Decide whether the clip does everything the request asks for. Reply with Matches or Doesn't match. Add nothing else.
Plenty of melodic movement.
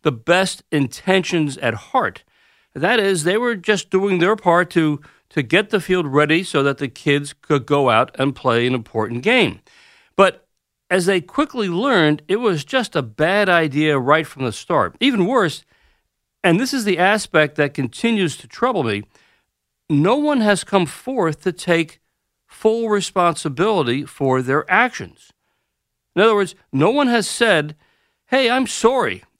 Matches